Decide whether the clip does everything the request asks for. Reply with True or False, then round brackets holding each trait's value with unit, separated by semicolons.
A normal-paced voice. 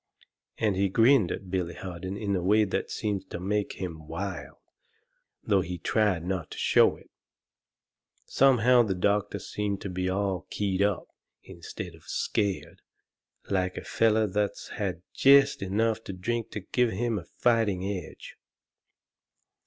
True (150 wpm)